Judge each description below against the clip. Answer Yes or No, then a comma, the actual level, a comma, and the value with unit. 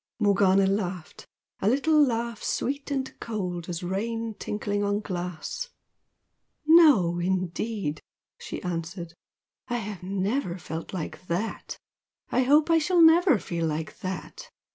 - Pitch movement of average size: No, wide, 6.2 semitones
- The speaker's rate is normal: No, slow, 125 wpm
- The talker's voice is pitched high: Yes, high, 205 Hz